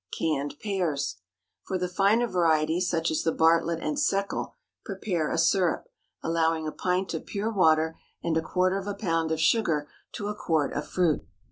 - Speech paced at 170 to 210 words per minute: Yes, average, 180 wpm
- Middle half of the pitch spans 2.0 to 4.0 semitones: Yes, average, 3.3 semitones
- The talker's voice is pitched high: No, medium, 170 Hz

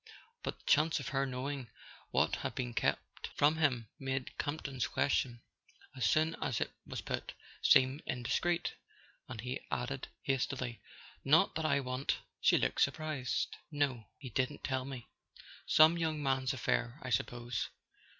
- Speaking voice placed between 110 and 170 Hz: Yes, low, 135 Hz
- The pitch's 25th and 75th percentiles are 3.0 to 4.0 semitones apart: No, narrow, 2.6 semitones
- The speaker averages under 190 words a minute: Yes, average, 150 wpm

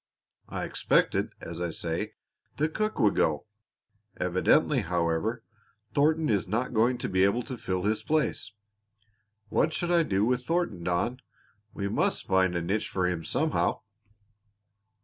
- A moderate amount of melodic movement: No, wide, 6.3 semitones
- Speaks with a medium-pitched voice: No, low, 105 Hz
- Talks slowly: No, average, 150 wpm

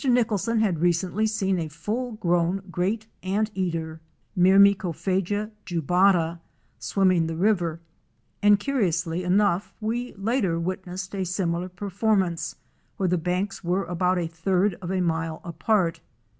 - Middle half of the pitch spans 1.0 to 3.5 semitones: Yes, average, 3.0 semitones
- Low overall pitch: No, medium, 185 Hz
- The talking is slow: Yes, slow, 125 wpm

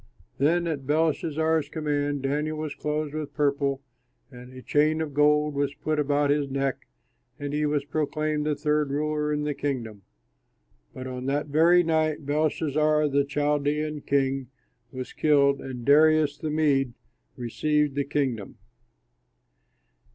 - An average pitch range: No, narrow, 1.6 semitones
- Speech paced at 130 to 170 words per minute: Yes, average, 140 wpm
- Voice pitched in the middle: Yes, medium, 145 Hz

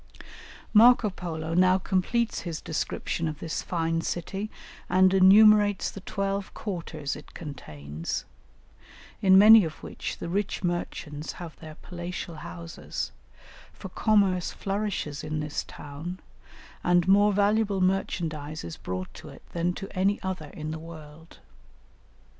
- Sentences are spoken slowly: Yes, slow, 130 wpm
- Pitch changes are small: No, average, 4.0 semitones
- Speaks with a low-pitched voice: No, medium, 175 Hz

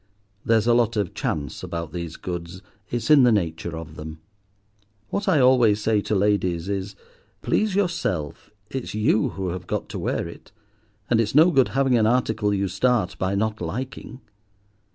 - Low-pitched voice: Yes, low, 105 Hz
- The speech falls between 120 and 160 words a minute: No, average, 170 wpm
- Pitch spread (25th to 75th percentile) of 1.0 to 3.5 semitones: No, wide, 5.6 semitones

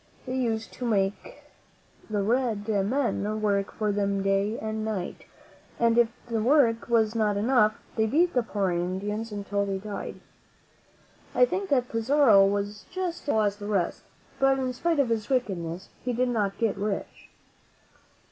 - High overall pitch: Yes, high, 215 Hz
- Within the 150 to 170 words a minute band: Yes, average, 165 wpm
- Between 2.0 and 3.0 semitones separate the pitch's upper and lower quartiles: No, average, 3.4 semitones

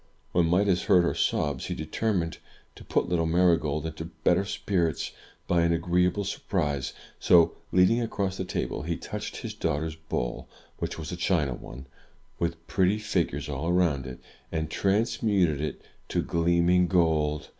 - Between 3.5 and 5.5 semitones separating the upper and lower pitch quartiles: No, average, 2.8 semitones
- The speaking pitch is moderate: No, very low, 85 Hz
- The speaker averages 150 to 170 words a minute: Yes, average, 155 wpm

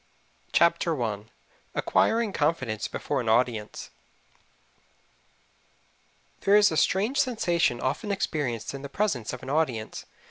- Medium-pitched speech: Yes, medium, 150 Hz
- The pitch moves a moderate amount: No, wide, 8.4 semitones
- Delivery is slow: Yes, slow, 115 wpm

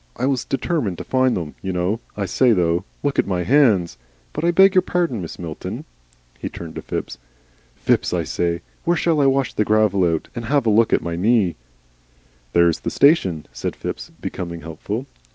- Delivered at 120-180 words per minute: No, average, 195 wpm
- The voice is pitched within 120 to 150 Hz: No, low, 105 Hz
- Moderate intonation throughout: No, wide, 7.9 semitones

